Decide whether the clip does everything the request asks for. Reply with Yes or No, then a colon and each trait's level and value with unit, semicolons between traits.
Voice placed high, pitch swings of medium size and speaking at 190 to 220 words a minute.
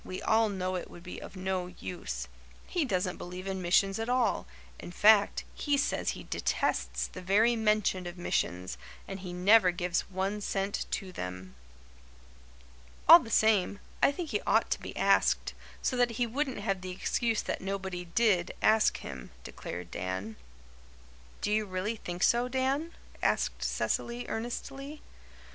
No: high, 195 Hz; average, 4.2 semitones; average, 160 wpm